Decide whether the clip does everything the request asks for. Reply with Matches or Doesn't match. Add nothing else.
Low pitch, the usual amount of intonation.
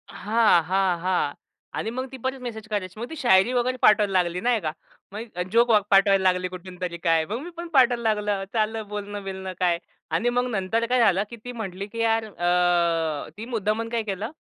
Doesn't match